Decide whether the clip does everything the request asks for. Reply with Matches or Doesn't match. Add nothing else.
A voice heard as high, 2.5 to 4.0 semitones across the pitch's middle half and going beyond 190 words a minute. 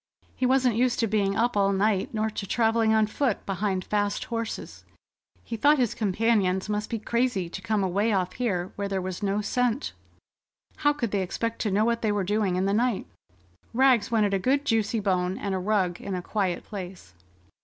Matches